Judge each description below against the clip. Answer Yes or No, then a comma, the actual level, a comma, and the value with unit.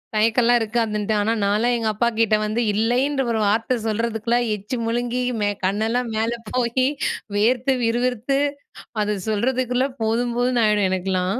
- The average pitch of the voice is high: Yes, high, 230 Hz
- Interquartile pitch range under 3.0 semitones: Yes, narrow, 2.5 semitones